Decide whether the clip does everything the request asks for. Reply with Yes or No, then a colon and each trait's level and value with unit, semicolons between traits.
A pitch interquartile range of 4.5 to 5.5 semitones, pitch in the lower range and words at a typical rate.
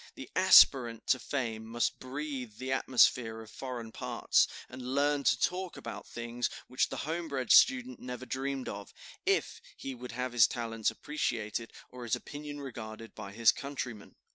No: average, 3.3 semitones; low, 125 Hz; average, 160 wpm